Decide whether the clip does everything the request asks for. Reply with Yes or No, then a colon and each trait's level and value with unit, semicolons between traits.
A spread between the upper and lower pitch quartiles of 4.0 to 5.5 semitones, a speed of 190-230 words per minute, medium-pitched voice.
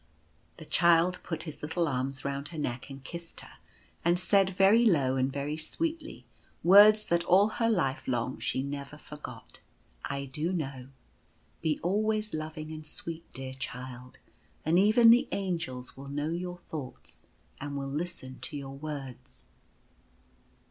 No: average, 4.8 semitones; average, 155 wpm; medium, 155 Hz